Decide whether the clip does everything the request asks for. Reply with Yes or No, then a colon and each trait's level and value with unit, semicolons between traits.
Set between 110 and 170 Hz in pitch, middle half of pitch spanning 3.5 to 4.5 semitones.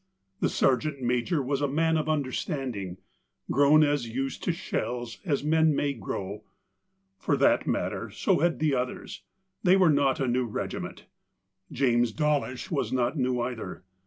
Yes: low, 135 Hz; average, 3.8 semitones